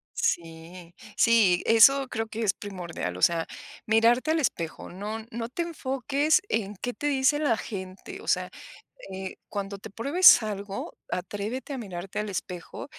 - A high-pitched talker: Yes, high, 220 Hz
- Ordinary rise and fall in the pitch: No, wide, 5.7 semitones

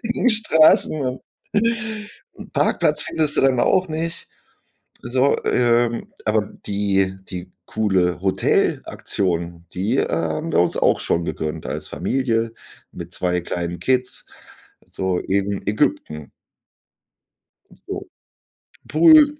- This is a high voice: No, low, 115 Hz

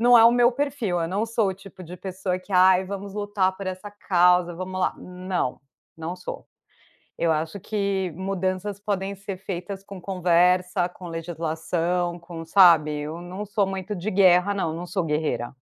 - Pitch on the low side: No, medium, 185 Hz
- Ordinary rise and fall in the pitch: No, narrow, 2.2 semitones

